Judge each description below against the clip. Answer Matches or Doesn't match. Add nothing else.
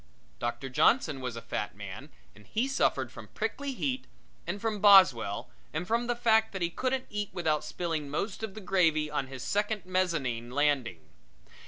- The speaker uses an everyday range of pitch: Doesn't match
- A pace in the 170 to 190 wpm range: Matches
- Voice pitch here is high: Doesn't match